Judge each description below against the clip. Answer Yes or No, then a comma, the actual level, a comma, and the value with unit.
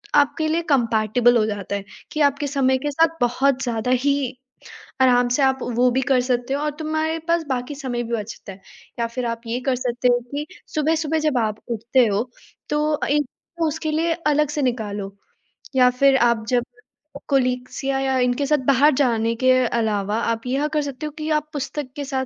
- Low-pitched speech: No, very high, 260 Hz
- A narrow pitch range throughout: No, average, 3.5 semitones